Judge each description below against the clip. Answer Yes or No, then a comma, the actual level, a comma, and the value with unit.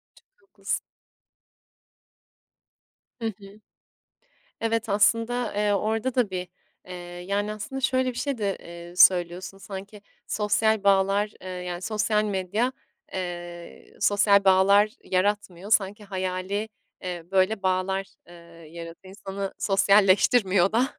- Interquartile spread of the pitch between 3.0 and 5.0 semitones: No, narrow, 2.4 semitones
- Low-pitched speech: No, high, 200 Hz